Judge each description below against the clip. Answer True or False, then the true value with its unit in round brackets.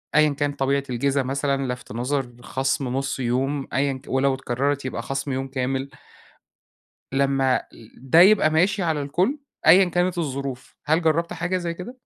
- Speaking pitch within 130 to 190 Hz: True (140 Hz)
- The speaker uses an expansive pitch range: False (3.3 semitones)